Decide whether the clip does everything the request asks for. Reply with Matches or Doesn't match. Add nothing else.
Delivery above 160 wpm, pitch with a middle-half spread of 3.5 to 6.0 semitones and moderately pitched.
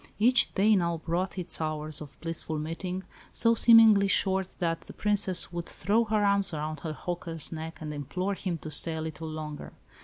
Matches